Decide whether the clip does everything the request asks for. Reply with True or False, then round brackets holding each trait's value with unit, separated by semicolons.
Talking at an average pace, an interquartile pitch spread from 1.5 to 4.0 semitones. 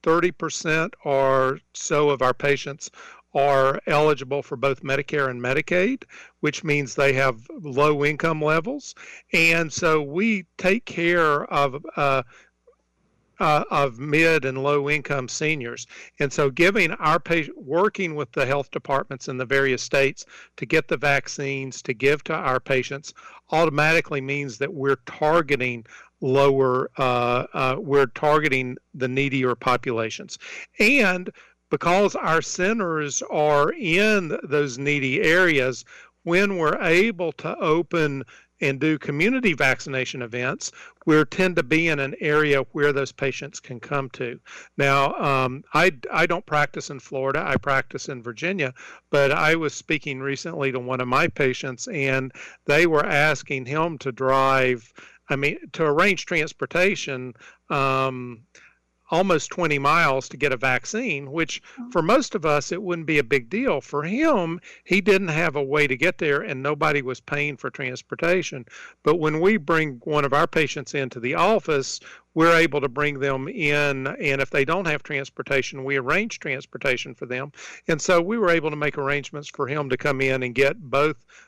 True (160 wpm; 3.2 semitones)